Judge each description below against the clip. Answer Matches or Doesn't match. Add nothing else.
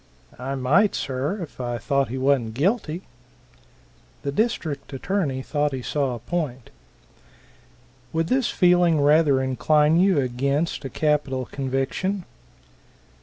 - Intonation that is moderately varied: Matches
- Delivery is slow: Matches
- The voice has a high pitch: Doesn't match